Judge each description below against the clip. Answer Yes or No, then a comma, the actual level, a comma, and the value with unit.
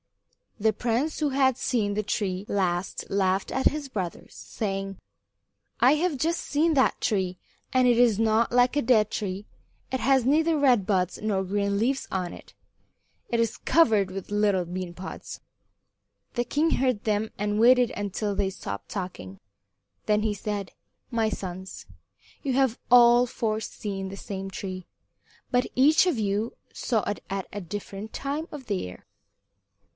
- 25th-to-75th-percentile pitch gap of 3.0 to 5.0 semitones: Yes, average, 4.4 semitones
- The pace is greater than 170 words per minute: No, average, 160 wpm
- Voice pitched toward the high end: Yes, high, 215 Hz